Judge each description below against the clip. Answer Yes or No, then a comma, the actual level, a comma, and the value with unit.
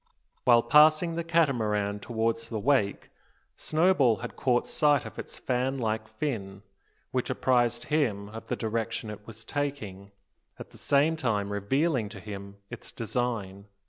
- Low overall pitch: Yes, low, 115 Hz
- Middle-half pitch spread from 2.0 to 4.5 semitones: No, average, 5.1 semitones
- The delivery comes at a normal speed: Yes, average, 145 wpm